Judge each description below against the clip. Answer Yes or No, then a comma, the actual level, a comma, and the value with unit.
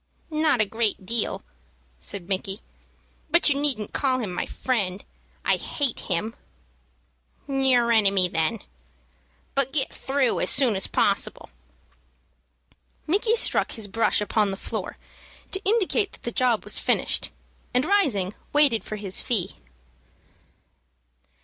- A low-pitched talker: No, high, 235 Hz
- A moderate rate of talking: No, slow, 130 wpm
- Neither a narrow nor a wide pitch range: No, wide, 5.7 semitones